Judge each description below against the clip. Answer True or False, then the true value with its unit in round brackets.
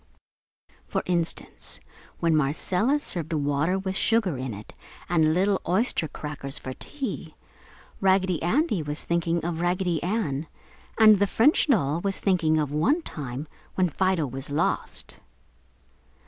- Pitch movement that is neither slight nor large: True (4.3 semitones)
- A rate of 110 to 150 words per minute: True (135 wpm)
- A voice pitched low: False (170 Hz)